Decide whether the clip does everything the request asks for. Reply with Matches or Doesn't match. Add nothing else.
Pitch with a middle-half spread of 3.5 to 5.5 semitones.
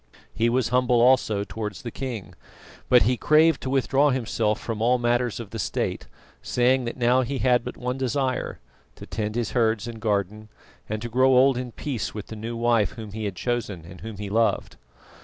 Doesn't match